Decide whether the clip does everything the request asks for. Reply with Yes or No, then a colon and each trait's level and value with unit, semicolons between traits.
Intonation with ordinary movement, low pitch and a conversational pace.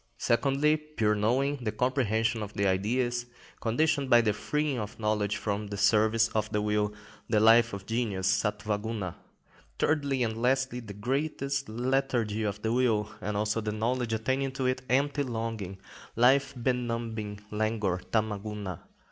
Yes: average, 3.4 semitones; low, 115 Hz; average, 155 wpm